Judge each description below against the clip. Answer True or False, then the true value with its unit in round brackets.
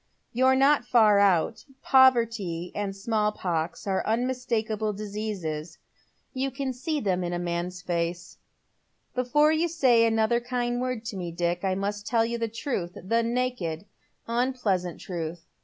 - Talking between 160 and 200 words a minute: False (150 wpm)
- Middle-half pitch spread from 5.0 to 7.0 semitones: True (5.6 semitones)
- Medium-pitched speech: False (220 Hz)